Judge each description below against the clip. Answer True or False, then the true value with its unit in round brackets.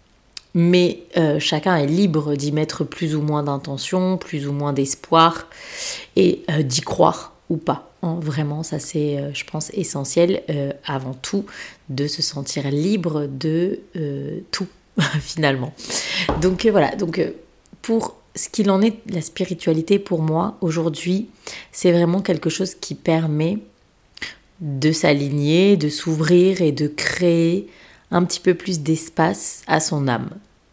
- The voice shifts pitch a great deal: False (3.7 semitones)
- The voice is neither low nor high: True (165 Hz)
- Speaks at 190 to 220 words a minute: False (145 wpm)